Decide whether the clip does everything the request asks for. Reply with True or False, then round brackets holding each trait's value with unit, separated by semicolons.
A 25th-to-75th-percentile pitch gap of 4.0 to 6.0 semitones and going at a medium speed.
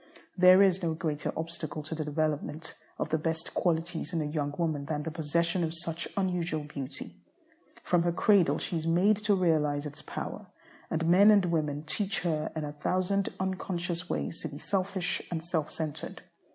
False (2.8 semitones; 180 wpm)